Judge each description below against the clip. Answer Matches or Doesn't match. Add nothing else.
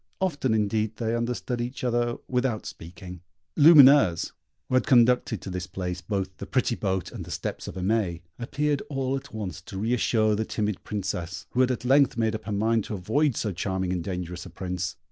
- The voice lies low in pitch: Matches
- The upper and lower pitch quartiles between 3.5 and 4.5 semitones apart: Doesn't match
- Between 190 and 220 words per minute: Matches